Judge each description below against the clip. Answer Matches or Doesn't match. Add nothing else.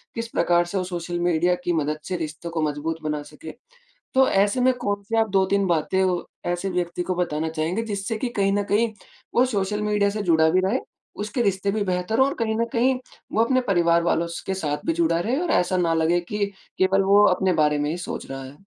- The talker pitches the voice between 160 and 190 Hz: Matches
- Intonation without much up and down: Doesn't match